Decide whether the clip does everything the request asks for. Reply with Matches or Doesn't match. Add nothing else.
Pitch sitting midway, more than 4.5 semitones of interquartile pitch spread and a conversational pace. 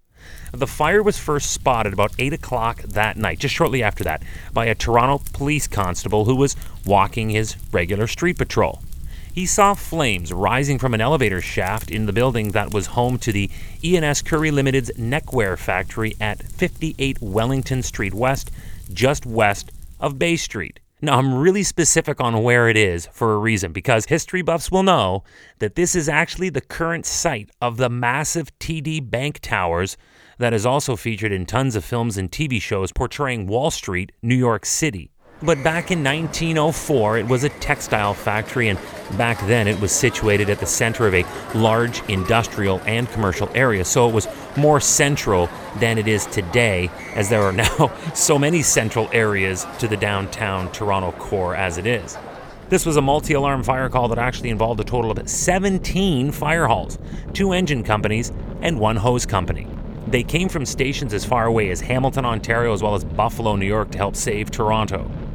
Doesn't match